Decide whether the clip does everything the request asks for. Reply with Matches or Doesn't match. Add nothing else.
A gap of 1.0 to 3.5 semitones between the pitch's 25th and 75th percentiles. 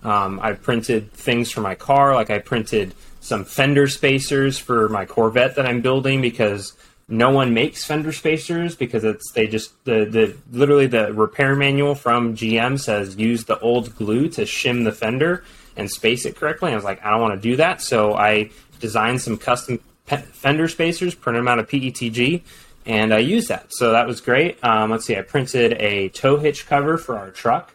Doesn't match